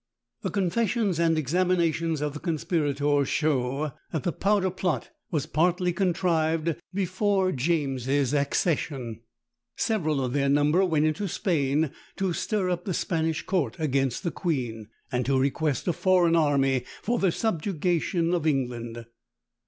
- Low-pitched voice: No, medium, 160 Hz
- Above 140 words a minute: No, slow, 135 wpm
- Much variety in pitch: No, average, 4.3 semitones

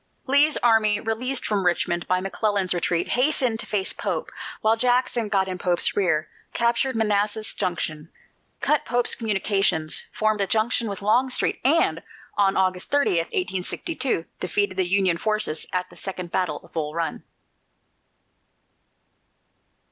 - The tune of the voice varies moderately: Yes, average, 4.0 semitones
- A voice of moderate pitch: No, high, 205 Hz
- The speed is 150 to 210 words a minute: No, slow, 135 wpm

